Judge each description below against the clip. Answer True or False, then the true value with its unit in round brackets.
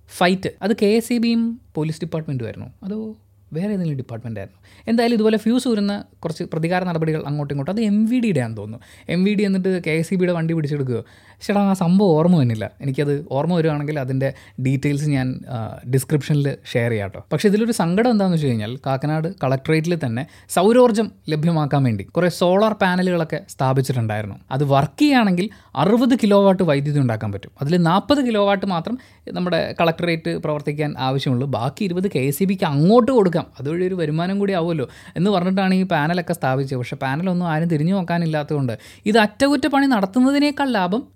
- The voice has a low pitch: False (165 Hz)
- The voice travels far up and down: True (6.6 semitones)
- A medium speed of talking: False (160 wpm)